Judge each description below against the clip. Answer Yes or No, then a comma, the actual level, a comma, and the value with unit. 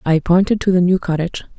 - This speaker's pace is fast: Yes, fast, 230 wpm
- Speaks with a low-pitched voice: No, medium, 180 Hz